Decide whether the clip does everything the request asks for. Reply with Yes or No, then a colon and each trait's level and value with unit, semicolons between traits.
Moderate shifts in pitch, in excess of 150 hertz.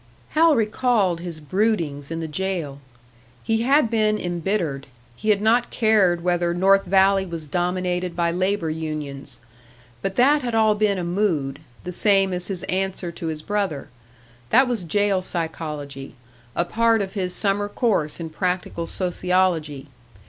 Yes: average, 3.9 semitones; medium, 185 Hz